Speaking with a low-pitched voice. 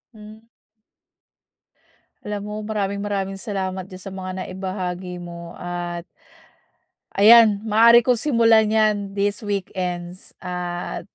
No: high, 195 Hz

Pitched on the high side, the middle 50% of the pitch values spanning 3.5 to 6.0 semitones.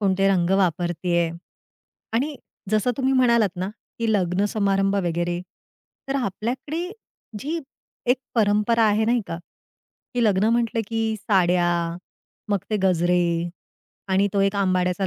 Yes: high, 200 Hz; average, 4.2 semitones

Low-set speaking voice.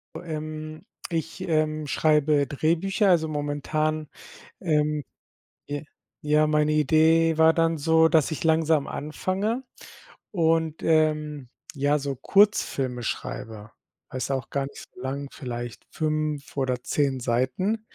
No: medium, 155 Hz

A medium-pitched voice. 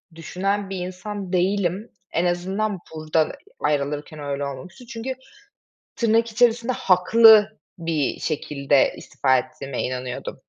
Yes: medium, 180 Hz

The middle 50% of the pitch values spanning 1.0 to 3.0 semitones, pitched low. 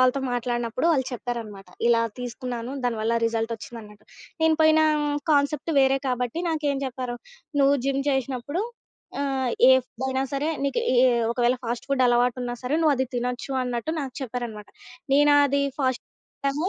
No: narrow, 2.5 semitones; very high, 255 Hz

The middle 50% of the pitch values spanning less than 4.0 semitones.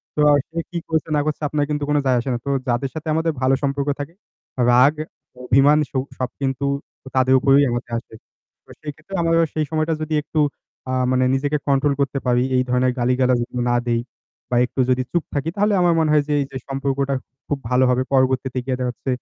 Yes: average, 2.9 semitones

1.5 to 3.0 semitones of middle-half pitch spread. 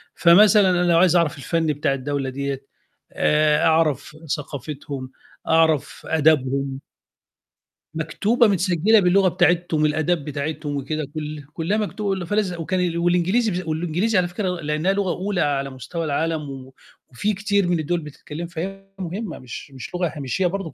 No: average, 3.8 semitones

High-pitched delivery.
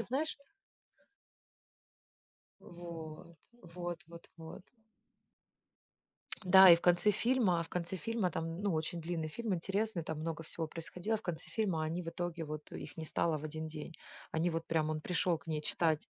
No: medium, 170 Hz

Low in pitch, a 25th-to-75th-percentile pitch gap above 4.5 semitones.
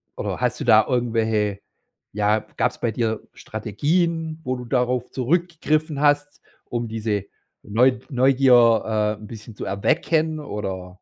Yes: low, 120 Hz; average, 5.1 semitones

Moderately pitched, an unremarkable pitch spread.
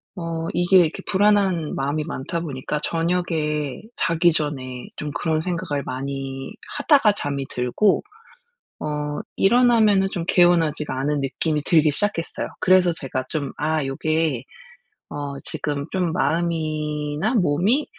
Yes: medium, 155 Hz; average, 3.5 semitones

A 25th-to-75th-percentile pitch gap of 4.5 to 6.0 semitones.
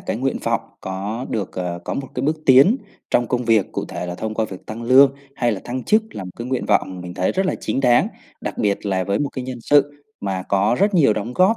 Yes: wide, 5.4 semitones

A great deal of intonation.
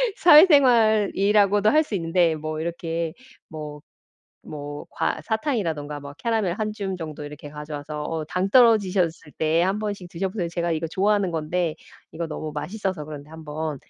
No: average, 4.9 semitones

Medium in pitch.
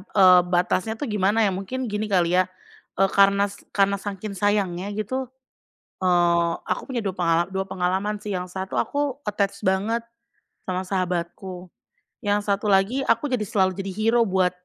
No: high, 195 Hz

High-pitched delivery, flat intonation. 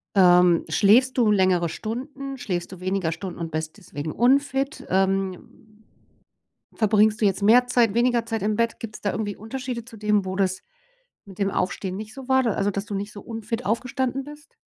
No: high, 210 Hz; average, 4.1 semitones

